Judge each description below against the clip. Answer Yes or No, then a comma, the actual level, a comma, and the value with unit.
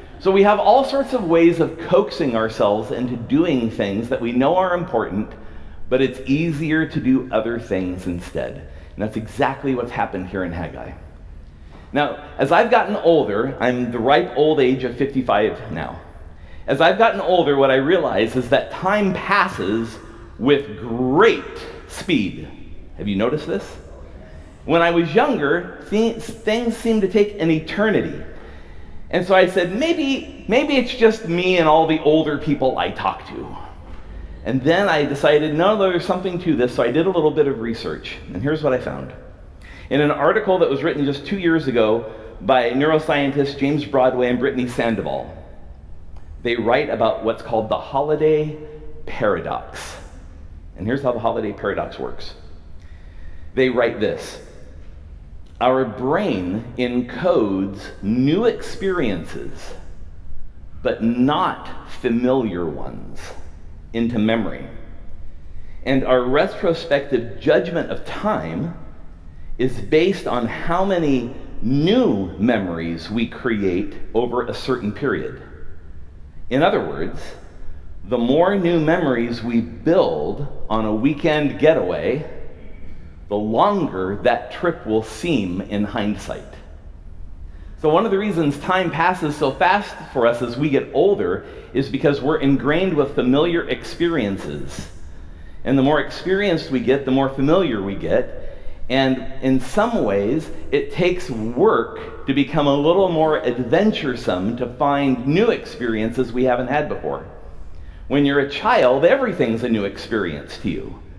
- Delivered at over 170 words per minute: No, average, 140 wpm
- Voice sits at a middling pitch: No, low, 125 Hz